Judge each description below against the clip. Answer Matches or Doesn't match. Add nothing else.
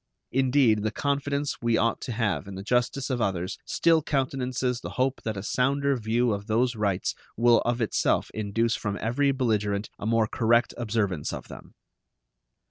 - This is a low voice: Matches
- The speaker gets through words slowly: Doesn't match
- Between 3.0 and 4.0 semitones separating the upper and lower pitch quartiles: Matches